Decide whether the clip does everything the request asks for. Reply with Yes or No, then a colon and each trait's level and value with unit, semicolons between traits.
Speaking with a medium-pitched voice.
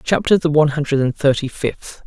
Yes: medium, 145 Hz